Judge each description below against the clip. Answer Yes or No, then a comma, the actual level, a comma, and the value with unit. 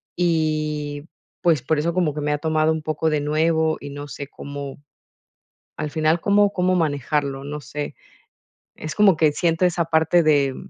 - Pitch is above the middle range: No, medium, 155 Hz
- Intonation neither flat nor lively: No, narrow, 2.2 semitones